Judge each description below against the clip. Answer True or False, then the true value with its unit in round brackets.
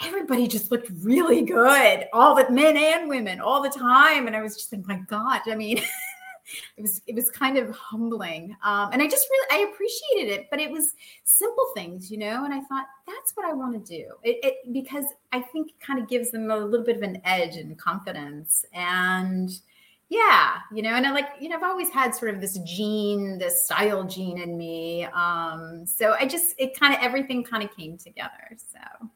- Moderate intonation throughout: False (6.1 semitones)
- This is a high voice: True (240 Hz)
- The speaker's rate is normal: False (220 wpm)